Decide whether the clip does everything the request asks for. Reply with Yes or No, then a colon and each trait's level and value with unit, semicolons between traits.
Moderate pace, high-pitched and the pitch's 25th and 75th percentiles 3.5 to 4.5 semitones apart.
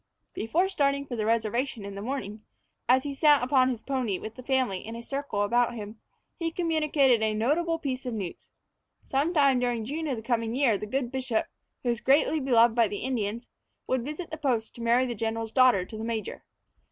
No: fast, 210 wpm; high, 245 Hz; average, 3.8 semitones